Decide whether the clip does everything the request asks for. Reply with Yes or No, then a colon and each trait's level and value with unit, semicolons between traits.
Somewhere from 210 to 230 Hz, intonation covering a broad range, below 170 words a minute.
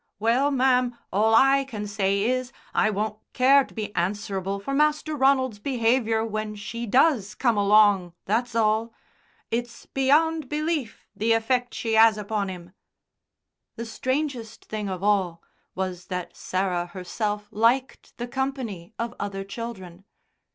No: high, 225 Hz; average, 4.1 semitones; average, 140 wpm